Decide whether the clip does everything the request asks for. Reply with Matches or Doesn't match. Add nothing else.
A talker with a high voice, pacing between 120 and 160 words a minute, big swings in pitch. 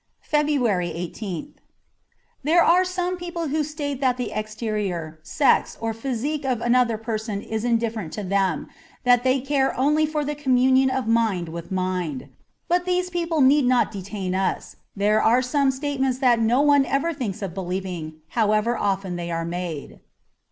Doesn't match